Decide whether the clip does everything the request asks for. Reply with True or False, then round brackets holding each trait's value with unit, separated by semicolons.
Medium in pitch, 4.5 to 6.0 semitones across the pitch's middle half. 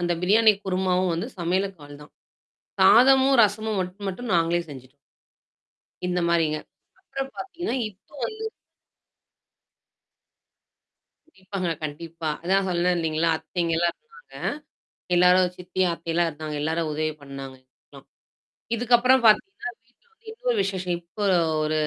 True (180 Hz; 4.9 semitones)